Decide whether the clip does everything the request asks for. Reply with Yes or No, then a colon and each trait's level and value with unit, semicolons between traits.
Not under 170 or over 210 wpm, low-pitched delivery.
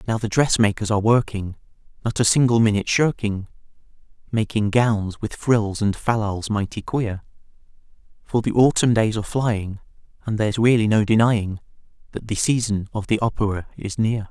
No: average, 160 wpm; low, 110 Hz